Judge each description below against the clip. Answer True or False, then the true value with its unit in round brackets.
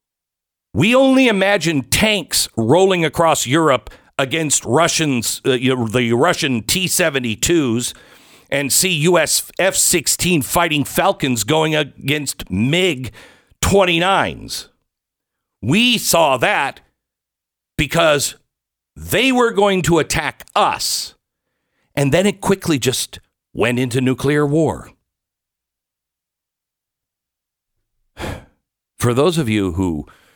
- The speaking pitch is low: False (155 Hz)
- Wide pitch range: True (6.2 semitones)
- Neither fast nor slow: False (95 wpm)